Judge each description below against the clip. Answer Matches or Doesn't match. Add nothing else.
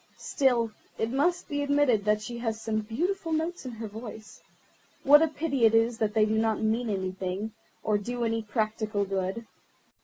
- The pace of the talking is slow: Doesn't match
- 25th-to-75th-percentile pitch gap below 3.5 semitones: Doesn't match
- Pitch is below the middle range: Doesn't match